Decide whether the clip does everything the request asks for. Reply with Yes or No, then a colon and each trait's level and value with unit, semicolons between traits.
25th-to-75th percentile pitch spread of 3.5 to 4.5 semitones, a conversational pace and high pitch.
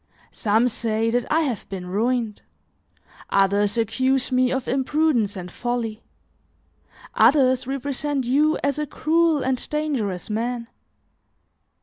No: average, 3.9 semitones; slow, 115 wpm; very high, 250 Hz